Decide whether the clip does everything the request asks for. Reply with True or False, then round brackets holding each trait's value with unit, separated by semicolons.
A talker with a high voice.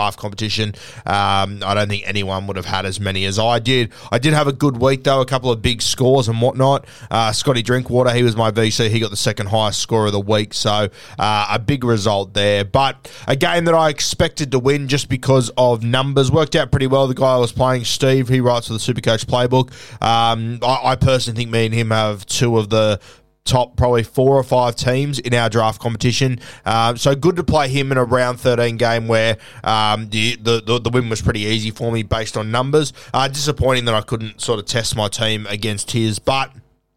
False (120 Hz)